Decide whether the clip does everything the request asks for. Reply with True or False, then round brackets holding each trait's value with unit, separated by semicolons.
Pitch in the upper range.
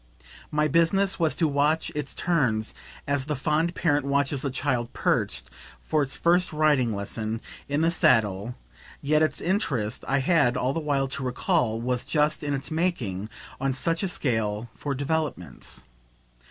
False (140 Hz)